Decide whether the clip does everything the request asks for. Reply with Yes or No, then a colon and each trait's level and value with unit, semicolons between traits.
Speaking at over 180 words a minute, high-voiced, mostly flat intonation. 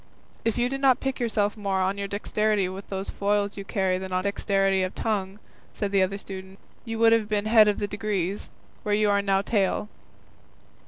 Yes: fast, 205 wpm; high, 200 Hz; narrow, 1.8 semitones